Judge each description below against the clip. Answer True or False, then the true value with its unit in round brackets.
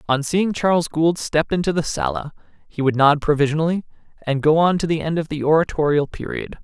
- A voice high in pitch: False (155 Hz)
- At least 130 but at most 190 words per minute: False (200 wpm)